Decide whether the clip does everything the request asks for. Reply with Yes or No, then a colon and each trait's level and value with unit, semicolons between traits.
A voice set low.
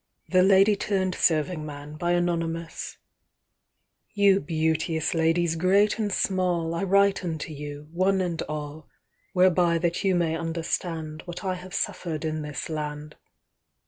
No: medium, 170 Hz